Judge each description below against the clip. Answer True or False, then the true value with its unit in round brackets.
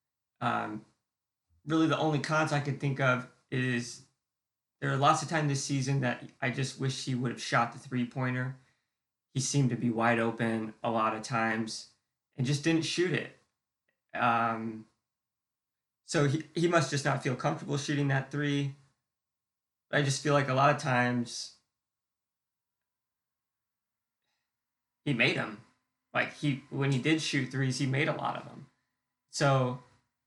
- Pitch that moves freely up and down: False (3.2 semitones)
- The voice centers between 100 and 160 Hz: True (130 Hz)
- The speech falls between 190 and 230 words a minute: False (160 wpm)